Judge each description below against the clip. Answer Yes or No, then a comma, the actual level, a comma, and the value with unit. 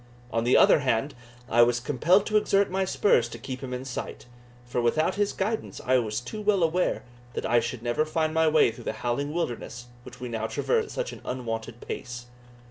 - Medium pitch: No, low, 130 Hz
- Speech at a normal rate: No, fast, 215 wpm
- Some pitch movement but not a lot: No, wide, 6.2 semitones